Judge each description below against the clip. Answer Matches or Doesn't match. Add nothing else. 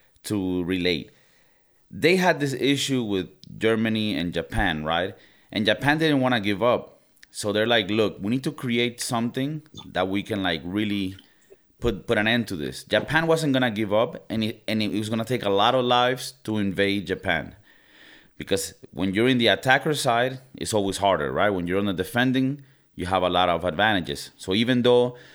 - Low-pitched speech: Matches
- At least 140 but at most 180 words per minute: Doesn't match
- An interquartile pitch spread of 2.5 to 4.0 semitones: Doesn't match